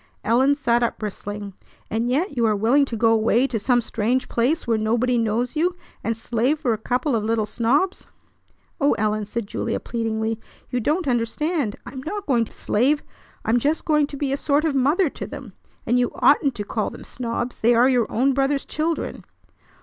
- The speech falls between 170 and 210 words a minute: Yes, average, 200 wpm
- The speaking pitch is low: No, high, 245 Hz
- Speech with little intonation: No, average, 3.9 semitones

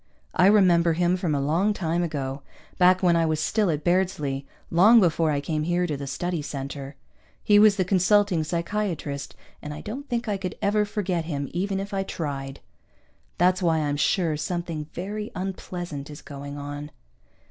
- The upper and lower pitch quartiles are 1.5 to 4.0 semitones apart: No, average, 4.4 semitones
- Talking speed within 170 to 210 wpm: Yes, average, 180 wpm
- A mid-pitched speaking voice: Yes, medium, 170 Hz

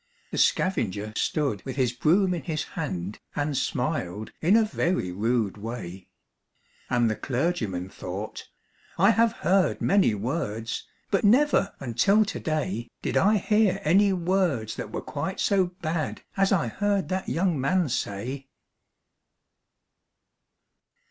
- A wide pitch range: Yes, wide, 9.0 semitones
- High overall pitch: No, medium, 150 Hz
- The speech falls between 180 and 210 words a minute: No, slow, 135 wpm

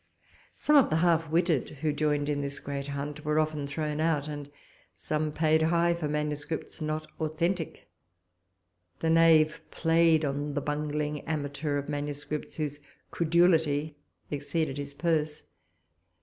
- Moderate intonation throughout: No, narrow, 1.8 semitones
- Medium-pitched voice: Yes, medium, 150 Hz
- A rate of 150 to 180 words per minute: No, slow, 135 wpm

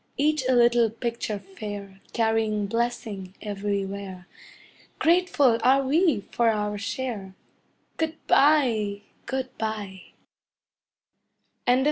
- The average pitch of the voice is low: No, high, 225 Hz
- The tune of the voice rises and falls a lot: No, average, 4.3 semitones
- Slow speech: Yes, slow, 95 wpm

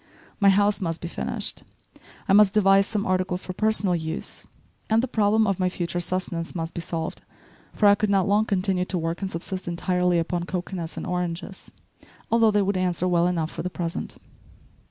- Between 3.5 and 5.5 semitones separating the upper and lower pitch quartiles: No, narrow, 2.6 semitones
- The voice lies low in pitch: No, medium, 185 Hz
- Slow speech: No, average, 190 wpm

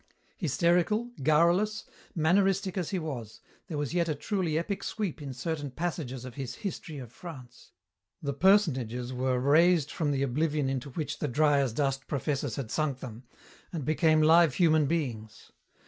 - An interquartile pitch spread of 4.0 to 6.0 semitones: Yes, average, 4.4 semitones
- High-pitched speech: No, medium, 150 Hz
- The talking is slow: No, average, 160 wpm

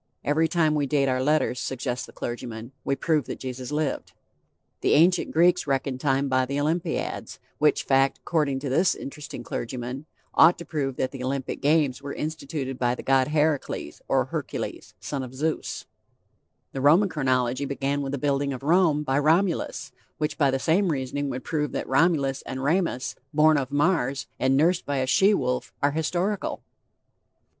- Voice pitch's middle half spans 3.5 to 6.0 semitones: No, average, 2.9 semitones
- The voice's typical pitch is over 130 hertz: Yes, medium, 140 Hz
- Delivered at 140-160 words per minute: No, average, 175 wpm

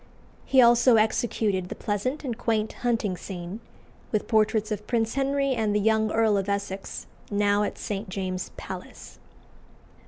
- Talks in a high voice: Yes, high, 215 Hz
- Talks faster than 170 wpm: No, average, 150 wpm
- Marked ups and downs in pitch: No, narrow, 2.5 semitones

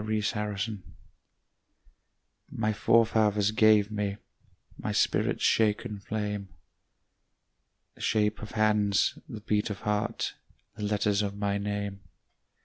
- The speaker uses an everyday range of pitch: No, narrow, 1.0 semitones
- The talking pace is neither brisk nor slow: No, slow, 105 wpm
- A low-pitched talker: Yes, low, 105 Hz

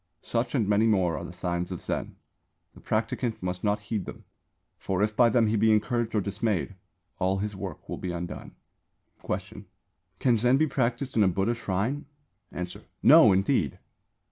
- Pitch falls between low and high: No, low, 105 Hz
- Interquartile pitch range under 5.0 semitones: Yes, average, 3.9 semitones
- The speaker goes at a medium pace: Yes, average, 175 wpm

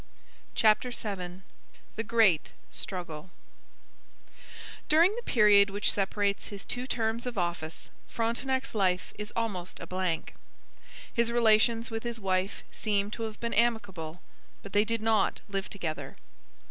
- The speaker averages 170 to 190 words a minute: No, slow, 135 wpm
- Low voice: No, high, 210 Hz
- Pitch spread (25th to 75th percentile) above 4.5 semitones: No, average, 3.5 semitones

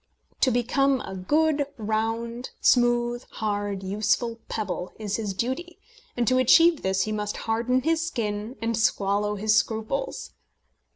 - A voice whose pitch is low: No, high, 225 Hz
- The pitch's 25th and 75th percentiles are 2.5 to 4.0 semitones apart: Yes, average, 3.6 semitones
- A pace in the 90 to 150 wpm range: Yes, slow, 135 wpm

